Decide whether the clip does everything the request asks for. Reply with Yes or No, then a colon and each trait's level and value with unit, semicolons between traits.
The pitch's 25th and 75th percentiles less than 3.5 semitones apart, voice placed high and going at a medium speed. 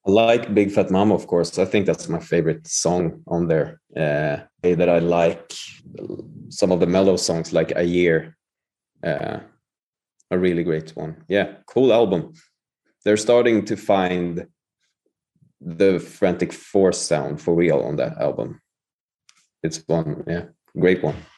No: narrow, 2.6 semitones; very low, 85 Hz; average, 150 wpm